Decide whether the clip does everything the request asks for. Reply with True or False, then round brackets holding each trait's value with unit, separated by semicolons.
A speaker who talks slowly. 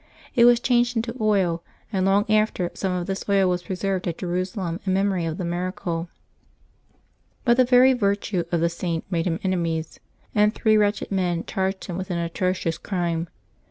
False (185 wpm)